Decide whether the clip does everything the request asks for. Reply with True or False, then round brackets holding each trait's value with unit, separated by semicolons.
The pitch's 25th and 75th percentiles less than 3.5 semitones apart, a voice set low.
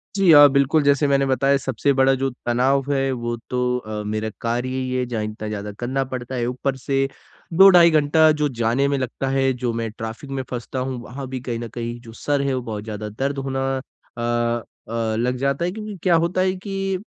True (2.9 semitones; 130 Hz)